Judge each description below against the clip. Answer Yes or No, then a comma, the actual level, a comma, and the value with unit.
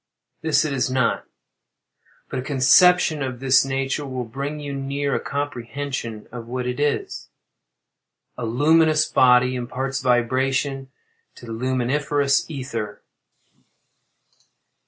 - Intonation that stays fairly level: Yes, narrow, 2.3 semitones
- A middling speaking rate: No, slow, 115 wpm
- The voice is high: No, low, 135 Hz